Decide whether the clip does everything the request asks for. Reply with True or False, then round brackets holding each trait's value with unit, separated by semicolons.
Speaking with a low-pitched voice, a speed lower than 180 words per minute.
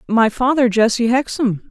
False (235 Hz; 140 wpm)